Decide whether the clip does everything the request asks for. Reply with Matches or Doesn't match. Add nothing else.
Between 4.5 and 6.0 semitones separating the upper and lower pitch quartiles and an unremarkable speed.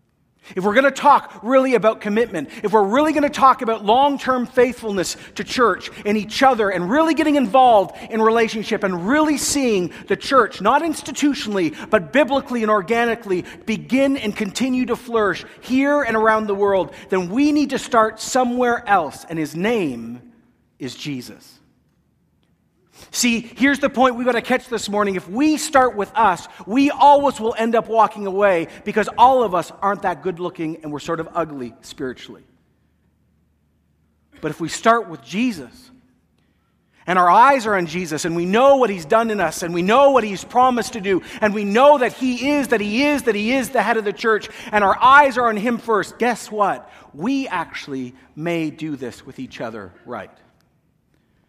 Matches